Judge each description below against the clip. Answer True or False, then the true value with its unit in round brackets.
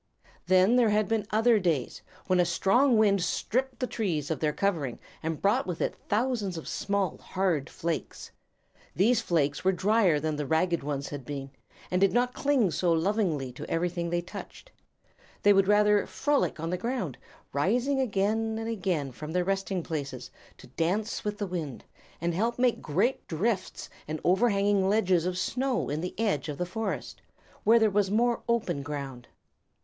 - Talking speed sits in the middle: True (175 wpm)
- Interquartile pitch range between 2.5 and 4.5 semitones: False (5.2 semitones)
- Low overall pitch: False (190 Hz)